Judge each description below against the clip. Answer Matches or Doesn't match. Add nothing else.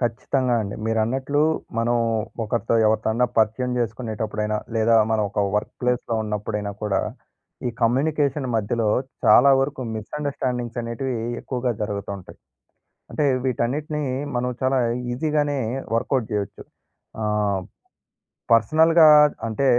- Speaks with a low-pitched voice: Matches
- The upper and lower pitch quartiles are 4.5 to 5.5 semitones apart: Doesn't match